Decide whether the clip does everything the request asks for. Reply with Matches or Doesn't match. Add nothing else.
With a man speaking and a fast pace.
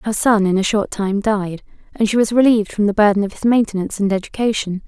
Doesn't match